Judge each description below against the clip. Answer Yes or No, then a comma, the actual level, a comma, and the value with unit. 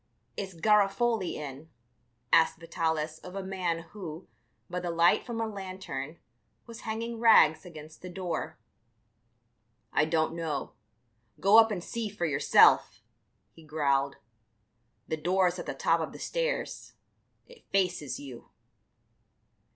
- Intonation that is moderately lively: Yes, average, 4.1 semitones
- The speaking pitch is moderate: Yes, medium, 175 Hz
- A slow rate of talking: Yes, slow, 130 wpm